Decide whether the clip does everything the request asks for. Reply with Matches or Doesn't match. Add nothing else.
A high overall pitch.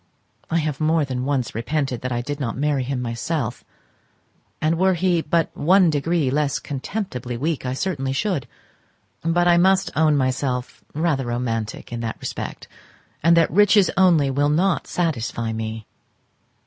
Doesn't match